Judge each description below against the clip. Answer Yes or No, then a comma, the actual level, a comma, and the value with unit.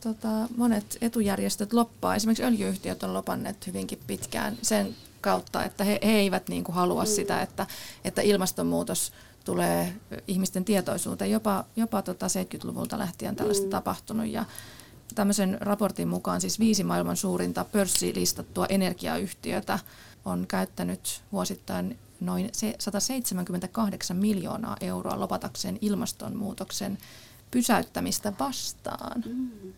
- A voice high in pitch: Yes, high, 200 Hz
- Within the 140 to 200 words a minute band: No, average, 105 wpm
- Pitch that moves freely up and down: No, average, 3.3 semitones